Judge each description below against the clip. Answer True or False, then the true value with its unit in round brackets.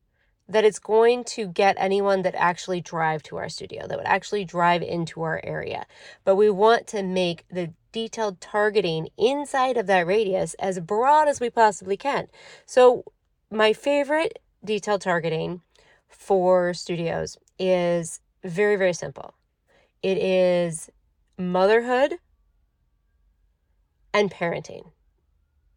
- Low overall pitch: False (190 Hz)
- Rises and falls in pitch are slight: False (4.2 semitones)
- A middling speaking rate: False (125 wpm)